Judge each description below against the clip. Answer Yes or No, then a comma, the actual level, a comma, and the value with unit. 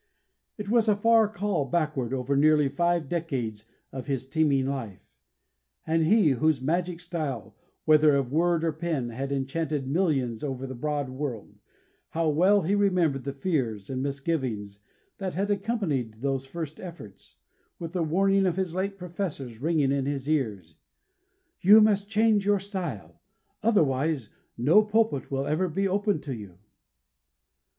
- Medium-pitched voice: Yes, medium, 155 Hz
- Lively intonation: Yes, wide, 5.7 semitones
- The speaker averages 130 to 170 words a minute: Yes, average, 150 wpm